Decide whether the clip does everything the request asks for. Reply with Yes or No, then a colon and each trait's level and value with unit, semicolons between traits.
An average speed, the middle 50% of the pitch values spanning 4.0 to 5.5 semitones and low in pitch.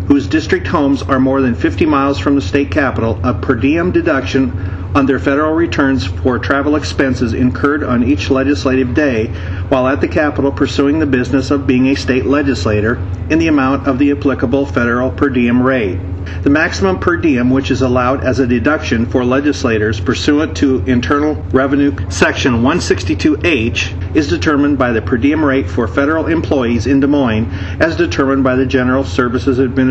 No: average, 175 wpm; average, 3.6 semitones; low, 130 Hz